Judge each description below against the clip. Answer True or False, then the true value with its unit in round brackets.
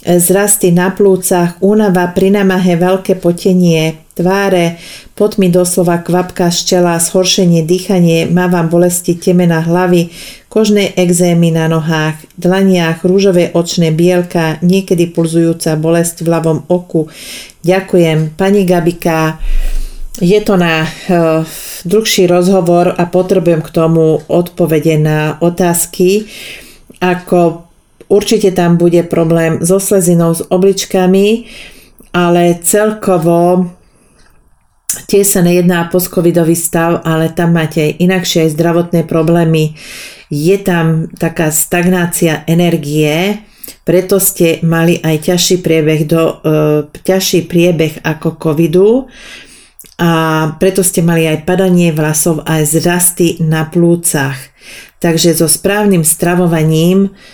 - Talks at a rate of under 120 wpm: True (110 wpm)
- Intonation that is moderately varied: False (2.1 semitones)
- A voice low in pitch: False (175 Hz)